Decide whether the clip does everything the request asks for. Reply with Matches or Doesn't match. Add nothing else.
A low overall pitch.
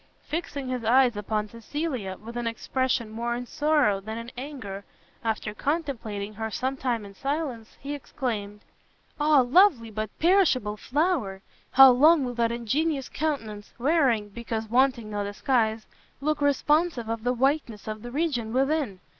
Doesn't match